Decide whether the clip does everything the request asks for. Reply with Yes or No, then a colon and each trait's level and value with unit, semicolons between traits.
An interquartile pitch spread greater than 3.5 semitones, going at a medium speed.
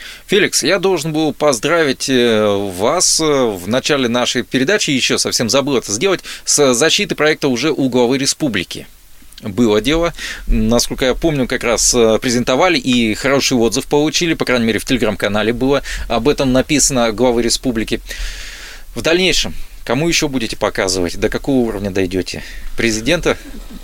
Yes: average, 4.2 semitones; average, 140 wpm